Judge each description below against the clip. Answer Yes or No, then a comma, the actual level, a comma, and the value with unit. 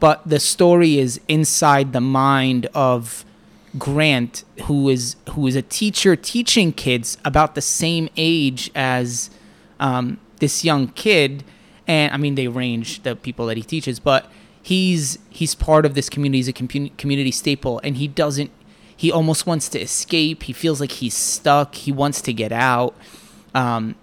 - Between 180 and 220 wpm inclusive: No, average, 165 wpm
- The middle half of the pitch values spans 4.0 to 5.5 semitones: No, average, 3.5 semitones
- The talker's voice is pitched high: No, medium, 140 Hz